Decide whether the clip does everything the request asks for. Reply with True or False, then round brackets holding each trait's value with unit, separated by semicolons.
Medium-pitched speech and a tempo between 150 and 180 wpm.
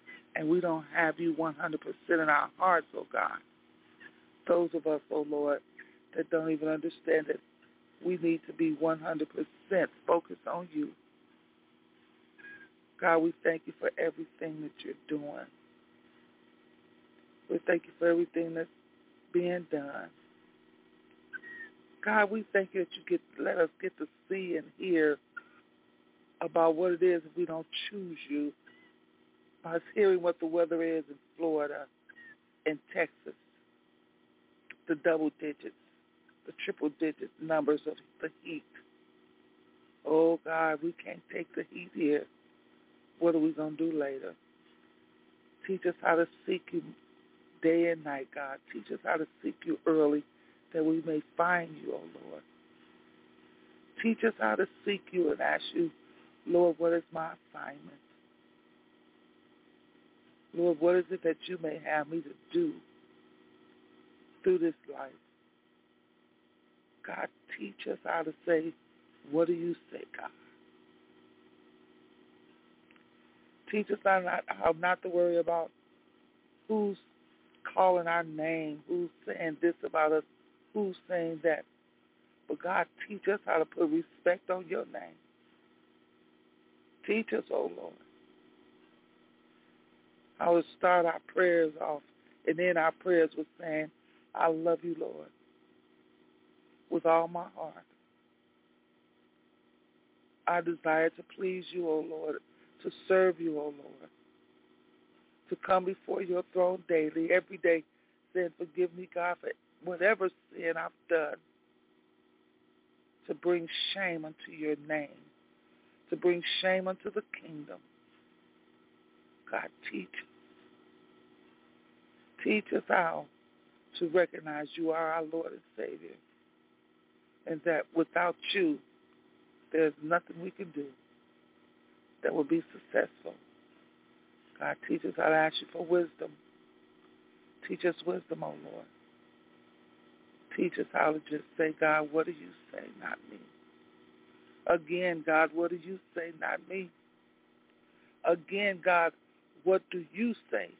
False (160 Hz; 135 wpm)